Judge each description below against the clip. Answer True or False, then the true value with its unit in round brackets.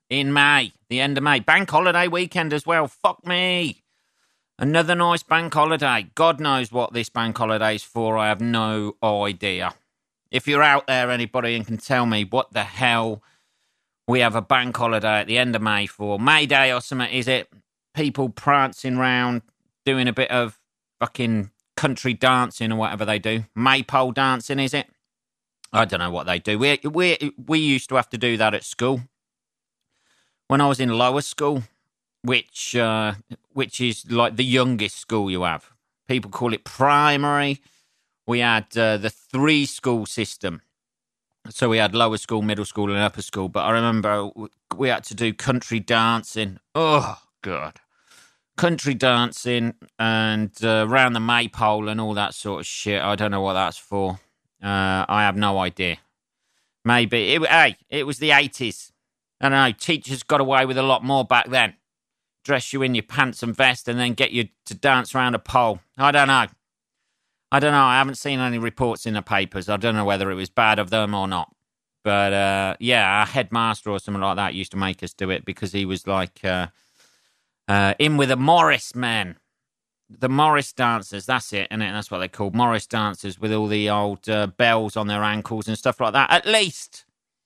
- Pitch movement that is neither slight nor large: True (4.1 semitones)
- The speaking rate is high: False (190 wpm)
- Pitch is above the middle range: False (115 Hz)